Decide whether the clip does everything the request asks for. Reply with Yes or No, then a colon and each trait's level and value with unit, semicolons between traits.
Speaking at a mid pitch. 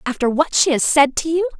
No: very high, 280 Hz